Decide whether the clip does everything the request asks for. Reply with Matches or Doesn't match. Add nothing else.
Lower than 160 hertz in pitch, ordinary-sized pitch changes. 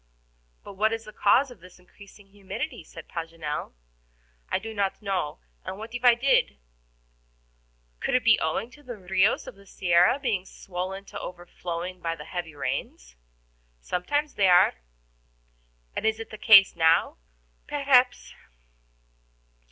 Doesn't match